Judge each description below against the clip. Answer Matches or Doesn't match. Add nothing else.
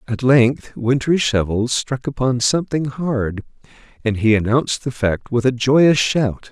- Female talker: Doesn't match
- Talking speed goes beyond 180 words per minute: Doesn't match